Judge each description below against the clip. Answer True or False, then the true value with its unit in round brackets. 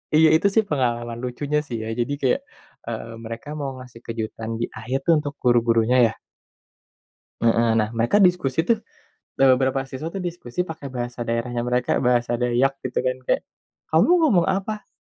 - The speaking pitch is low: True (125 Hz)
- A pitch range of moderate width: True (4.4 semitones)